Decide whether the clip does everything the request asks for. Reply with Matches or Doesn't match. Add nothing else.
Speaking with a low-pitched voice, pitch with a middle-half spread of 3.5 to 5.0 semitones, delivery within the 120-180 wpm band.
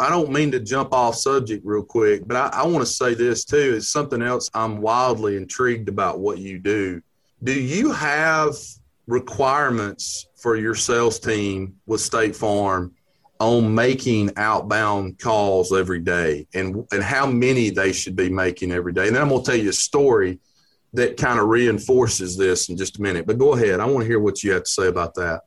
Doesn't match